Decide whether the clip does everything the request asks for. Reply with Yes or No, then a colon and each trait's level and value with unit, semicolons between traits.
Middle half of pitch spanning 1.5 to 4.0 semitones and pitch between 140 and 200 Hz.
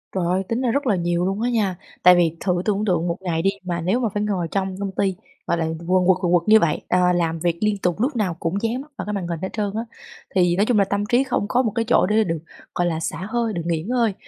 Yes: average, 3.7 semitones; high, 190 Hz